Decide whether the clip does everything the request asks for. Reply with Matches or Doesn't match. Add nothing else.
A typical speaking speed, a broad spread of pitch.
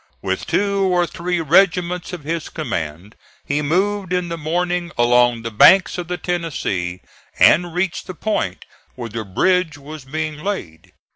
Matches